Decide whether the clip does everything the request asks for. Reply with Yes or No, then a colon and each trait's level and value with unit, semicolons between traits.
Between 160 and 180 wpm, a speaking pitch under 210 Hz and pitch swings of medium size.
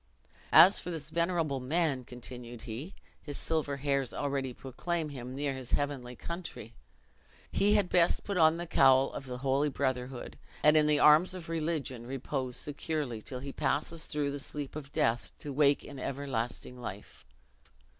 Yes: average, 165 wpm; medium, 140 Hz; average, 3.5 semitones